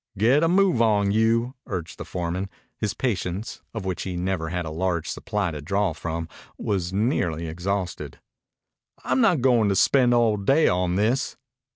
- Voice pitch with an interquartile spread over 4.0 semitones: Yes, average, 4.8 semitones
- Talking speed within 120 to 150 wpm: No, average, 170 wpm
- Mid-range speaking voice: No, low, 100 Hz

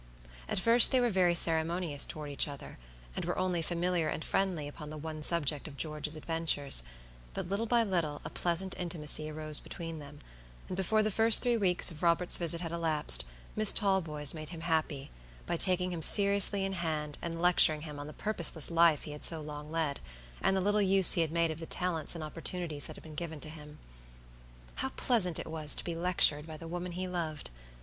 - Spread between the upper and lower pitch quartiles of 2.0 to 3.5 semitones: Yes, average, 3.0 semitones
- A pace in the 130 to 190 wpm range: No, fast, 205 wpm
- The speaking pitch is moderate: Yes, medium, 165 Hz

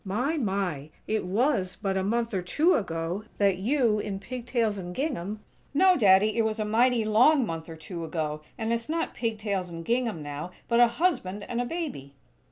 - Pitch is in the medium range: No, high, 215 Hz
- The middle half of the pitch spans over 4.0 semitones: Yes, average, 4.8 semitones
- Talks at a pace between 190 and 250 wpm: Yes, fast, 205 wpm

